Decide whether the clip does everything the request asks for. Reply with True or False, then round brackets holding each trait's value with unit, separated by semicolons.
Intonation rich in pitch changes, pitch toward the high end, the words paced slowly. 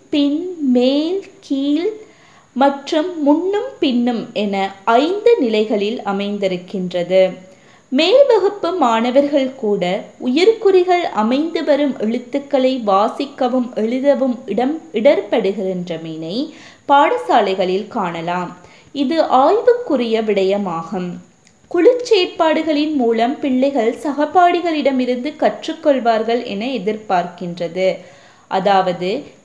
True (7.5 semitones; 255 Hz; 70 wpm)